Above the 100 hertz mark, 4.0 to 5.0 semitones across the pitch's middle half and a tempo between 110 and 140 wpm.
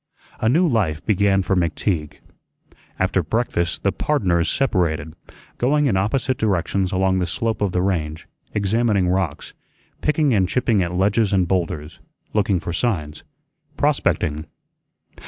No: very low, 95 Hz; average, 4.3 semitones; slow, 135 wpm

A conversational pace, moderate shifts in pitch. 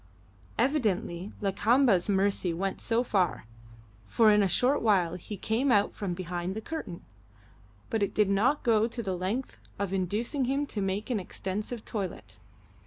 Yes: average, 160 wpm; average, 3.8 semitones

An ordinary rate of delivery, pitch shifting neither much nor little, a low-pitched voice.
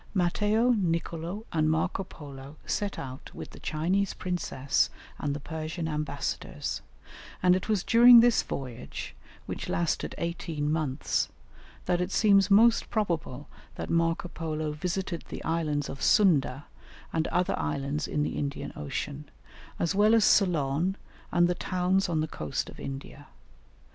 No: average, 145 wpm; average, 4.3 semitones; medium, 165 Hz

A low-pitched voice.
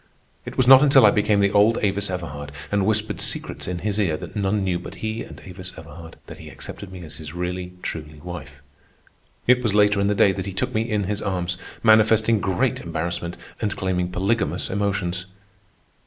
Yes: very low, 95 Hz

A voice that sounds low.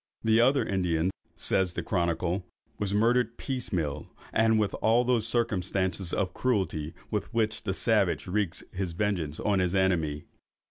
Yes: very low, 95 Hz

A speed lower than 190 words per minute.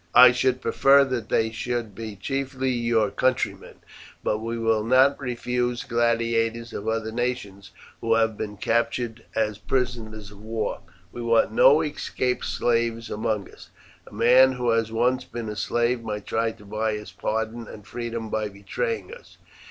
Yes: average, 160 wpm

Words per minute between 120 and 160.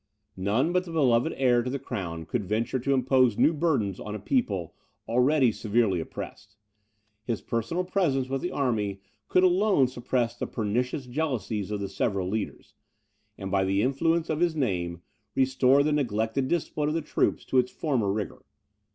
No: average, 170 wpm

